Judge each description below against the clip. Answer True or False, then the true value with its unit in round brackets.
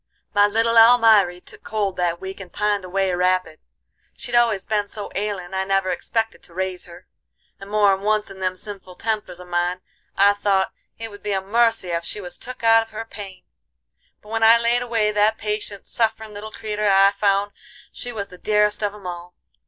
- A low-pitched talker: False (205 Hz)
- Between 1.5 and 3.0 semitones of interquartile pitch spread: True (2.5 semitones)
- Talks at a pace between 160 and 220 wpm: True (200 wpm)